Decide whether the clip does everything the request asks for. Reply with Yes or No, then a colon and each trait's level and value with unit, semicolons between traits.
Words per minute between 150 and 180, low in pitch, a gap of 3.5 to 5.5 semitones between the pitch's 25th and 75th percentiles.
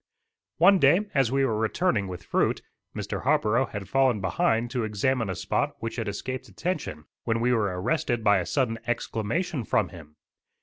Yes: average, 175 wpm; low, 115 Hz; average, 4.4 semitones